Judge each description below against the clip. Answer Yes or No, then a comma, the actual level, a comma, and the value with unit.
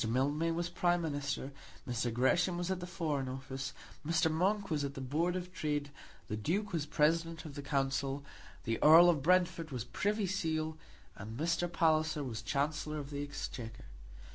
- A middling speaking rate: Yes, average, 170 wpm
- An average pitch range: Yes, average, 3.8 semitones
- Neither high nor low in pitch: Yes, medium, 155 Hz